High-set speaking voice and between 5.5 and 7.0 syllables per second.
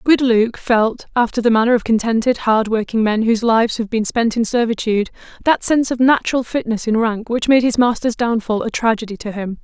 Yes: high, 230 Hz; 5.7 syllables/s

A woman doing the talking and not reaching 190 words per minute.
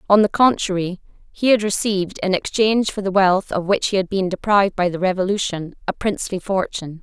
No: female; average, 195 wpm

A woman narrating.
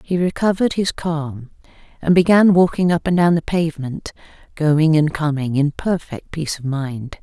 Yes: female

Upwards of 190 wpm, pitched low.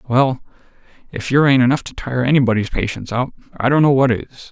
Yes: average, 200 wpm; low, 130 Hz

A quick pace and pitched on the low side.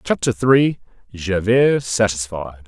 No: slow, 65 wpm; low, 105 Hz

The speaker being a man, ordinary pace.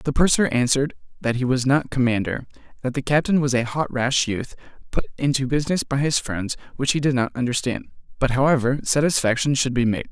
Yes: male; average, 195 wpm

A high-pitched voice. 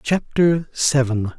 No: medium, 140 Hz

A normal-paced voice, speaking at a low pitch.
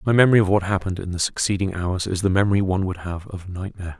No: fast, 255 wpm; very low, 95 Hz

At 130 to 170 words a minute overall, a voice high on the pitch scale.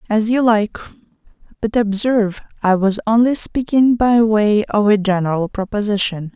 Yes: average, 140 wpm; high, 215 Hz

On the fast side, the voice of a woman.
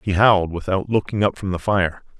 No: fast, 220 wpm; male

